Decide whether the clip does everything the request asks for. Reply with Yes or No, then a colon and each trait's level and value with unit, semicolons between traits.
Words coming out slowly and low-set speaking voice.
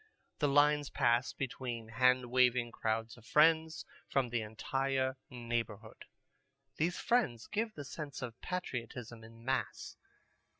Yes: slow, 125 wpm; low, 125 Hz